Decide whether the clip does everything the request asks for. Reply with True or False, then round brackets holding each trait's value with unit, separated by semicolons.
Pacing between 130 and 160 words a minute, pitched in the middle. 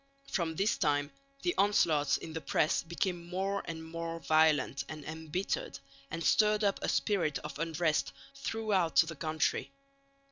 True (145 wpm; 165 Hz)